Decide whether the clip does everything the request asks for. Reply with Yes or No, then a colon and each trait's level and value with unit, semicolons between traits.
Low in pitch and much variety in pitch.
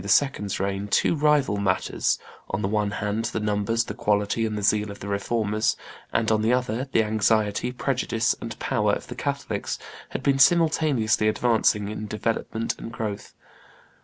No: low, 110 Hz; narrow, 2.4 semitones